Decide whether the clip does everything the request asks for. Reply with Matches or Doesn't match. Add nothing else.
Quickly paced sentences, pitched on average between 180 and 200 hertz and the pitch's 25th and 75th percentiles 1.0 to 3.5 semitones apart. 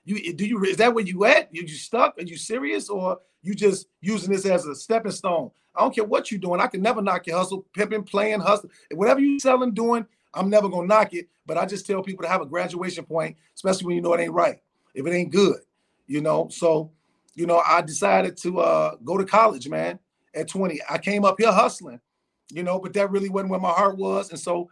Matches